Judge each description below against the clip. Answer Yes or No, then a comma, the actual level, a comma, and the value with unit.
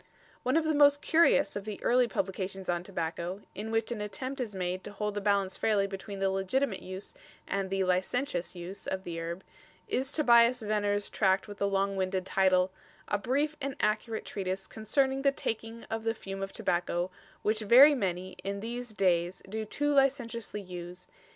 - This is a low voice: No, high, 205 Hz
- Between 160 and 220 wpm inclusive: Yes, average, 185 wpm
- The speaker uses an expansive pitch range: No, average, 3.9 semitones